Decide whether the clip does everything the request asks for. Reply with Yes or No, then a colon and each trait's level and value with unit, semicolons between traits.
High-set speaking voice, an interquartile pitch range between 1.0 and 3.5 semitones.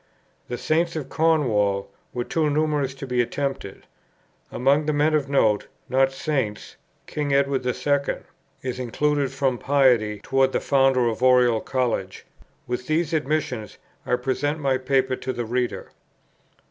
No: low, 135 Hz; average, 2.8 semitones